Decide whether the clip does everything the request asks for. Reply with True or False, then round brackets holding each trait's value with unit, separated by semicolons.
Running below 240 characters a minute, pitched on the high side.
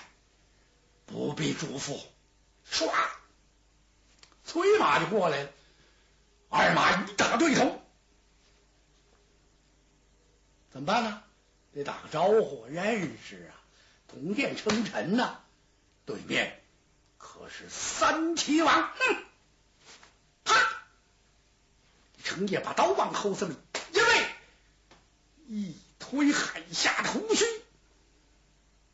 True (125 characters per minute; 320 Hz)